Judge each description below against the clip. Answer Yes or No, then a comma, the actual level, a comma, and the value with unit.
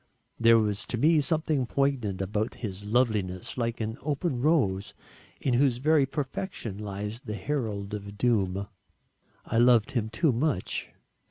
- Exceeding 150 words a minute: No, average, 145 wpm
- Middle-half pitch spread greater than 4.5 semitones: Yes, average, 5.0 semitones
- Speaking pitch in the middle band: No, low, 115 Hz